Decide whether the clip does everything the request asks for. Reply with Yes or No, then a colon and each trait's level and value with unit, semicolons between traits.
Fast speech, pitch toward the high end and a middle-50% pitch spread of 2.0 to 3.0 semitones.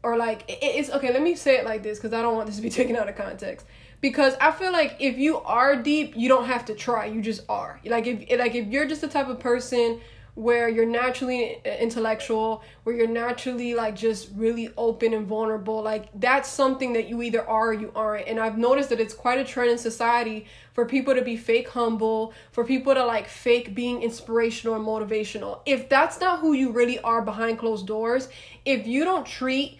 Yes: fast, 220 wpm; high, 235 Hz; average, 2.7 semitones